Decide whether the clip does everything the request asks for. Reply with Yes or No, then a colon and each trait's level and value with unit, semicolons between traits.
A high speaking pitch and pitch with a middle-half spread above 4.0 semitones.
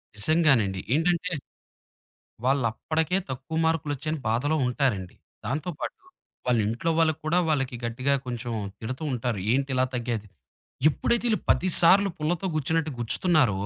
No: medium, 140 Hz; average, 5.0 semitones